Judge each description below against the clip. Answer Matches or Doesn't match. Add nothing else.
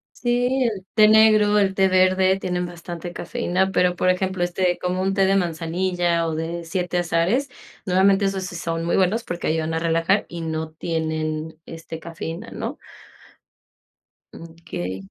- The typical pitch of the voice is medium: Matches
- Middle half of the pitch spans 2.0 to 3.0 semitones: Matches